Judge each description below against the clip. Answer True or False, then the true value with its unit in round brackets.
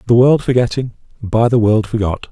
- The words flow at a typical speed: True (180 wpm)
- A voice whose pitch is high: False (115 Hz)